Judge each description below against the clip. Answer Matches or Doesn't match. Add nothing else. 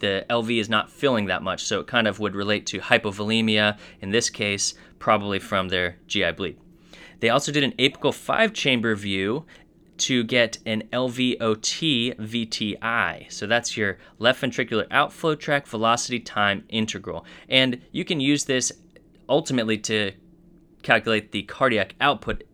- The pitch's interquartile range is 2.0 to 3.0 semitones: Doesn't match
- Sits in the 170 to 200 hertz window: Doesn't match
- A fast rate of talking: Doesn't match